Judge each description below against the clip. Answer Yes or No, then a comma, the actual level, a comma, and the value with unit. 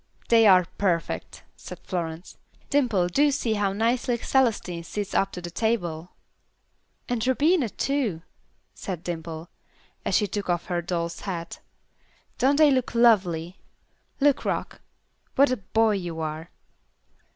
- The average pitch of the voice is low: No, high, 195 Hz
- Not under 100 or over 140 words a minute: Yes, slow, 135 wpm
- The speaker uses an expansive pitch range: Yes, wide, 5.8 semitones